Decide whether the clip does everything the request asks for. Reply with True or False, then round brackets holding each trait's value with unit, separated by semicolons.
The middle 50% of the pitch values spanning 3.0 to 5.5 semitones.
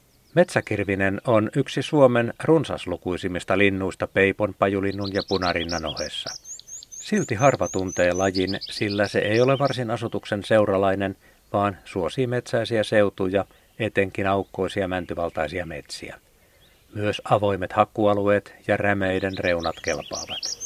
False (2.4 semitones)